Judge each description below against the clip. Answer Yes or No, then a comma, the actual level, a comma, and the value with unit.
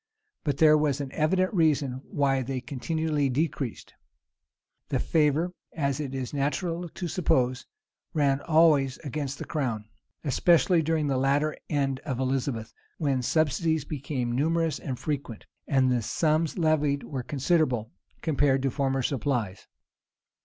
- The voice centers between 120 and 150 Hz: Yes, medium, 140 Hz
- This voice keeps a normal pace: No, slow, 130 wpm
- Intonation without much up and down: No, average, 3.0 semitones